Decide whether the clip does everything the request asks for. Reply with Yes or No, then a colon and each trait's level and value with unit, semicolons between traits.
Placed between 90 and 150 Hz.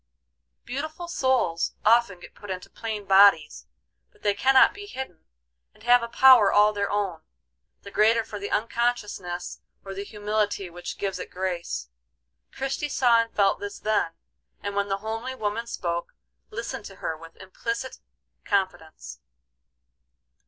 No: high, 205 Hz